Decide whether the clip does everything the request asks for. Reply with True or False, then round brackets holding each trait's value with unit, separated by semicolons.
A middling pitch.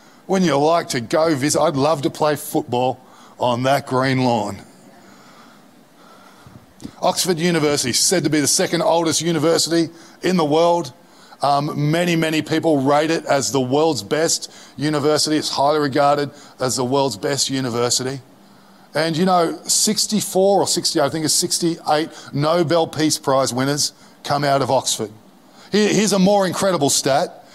True (155 Hz)